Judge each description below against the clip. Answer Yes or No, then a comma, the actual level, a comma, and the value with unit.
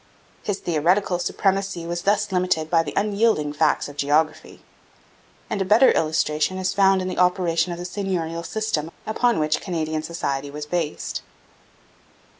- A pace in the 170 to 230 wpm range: No, average, 150 wpm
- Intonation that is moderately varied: Yes, average, 3.7 semitones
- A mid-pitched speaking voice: Yes, medium, 175 Hz